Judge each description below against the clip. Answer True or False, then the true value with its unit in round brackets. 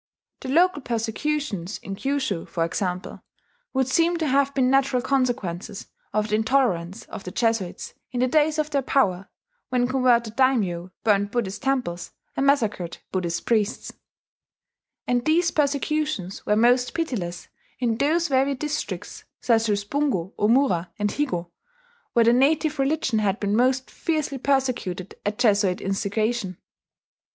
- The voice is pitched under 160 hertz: False (240 Hz)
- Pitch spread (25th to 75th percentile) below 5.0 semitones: False (5.4 semitones)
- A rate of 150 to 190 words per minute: False (140 wpm)